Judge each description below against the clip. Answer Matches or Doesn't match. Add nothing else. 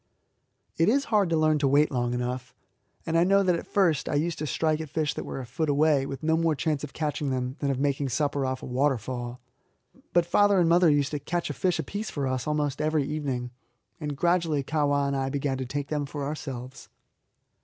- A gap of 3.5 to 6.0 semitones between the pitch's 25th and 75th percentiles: Doesn't match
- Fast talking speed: Matches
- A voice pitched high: Doesn't match